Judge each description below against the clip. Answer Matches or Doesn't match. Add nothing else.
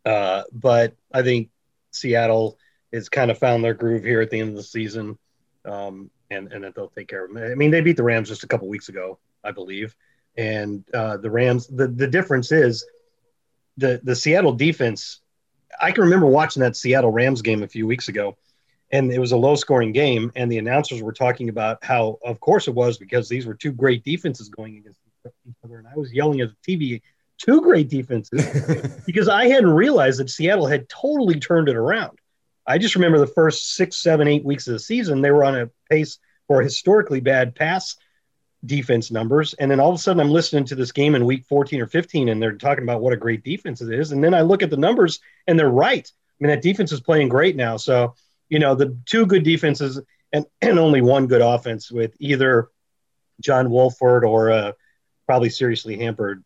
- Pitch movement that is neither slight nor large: Matches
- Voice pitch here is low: Matches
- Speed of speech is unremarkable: Doesn't match